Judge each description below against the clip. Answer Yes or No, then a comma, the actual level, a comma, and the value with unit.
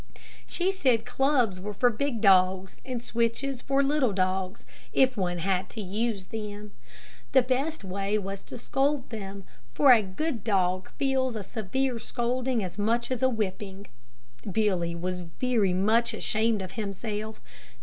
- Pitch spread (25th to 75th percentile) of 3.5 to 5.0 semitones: Yes, average, 4.6 semitones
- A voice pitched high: Yes, high, 220 Hz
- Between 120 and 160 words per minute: Yes, average, 150 wpm